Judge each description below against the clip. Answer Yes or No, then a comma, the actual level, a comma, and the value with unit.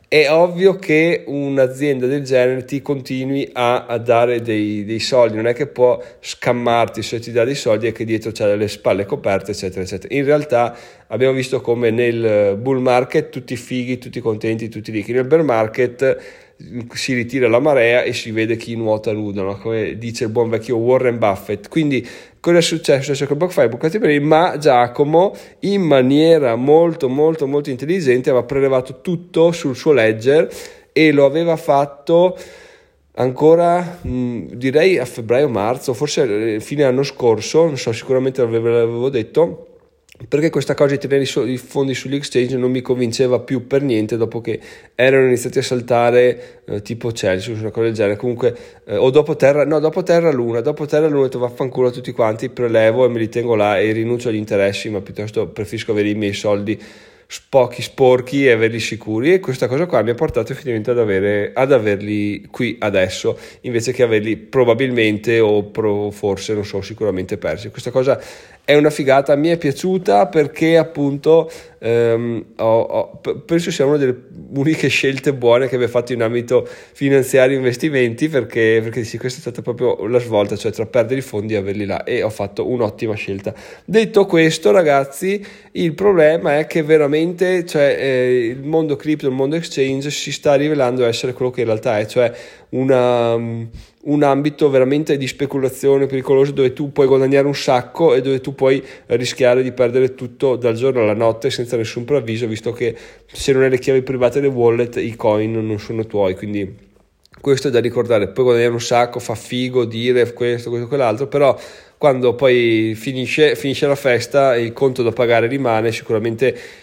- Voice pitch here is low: Yes, low, 125 Hz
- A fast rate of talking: Yes, fast, 180 wpm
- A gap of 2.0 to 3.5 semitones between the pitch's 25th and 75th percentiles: No, average, 3.9 semitones